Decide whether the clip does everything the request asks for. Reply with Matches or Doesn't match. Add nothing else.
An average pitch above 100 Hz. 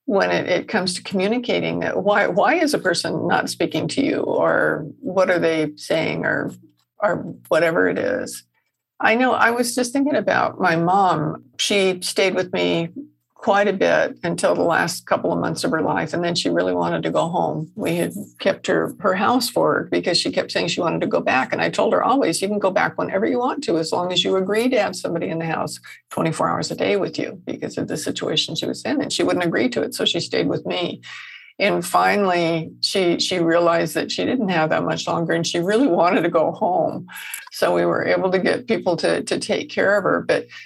Matches